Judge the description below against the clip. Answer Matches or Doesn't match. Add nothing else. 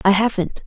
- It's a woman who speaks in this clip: Matches